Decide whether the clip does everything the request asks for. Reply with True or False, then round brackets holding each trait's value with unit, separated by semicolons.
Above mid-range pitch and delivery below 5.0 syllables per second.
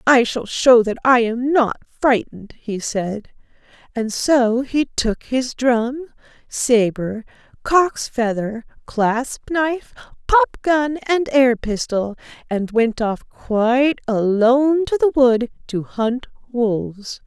True (245 Hz; 3.4 syllables/s)